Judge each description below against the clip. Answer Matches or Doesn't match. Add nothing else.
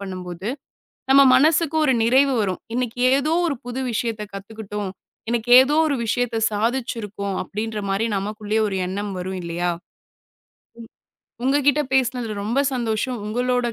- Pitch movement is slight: Doesn't match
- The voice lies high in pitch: Matches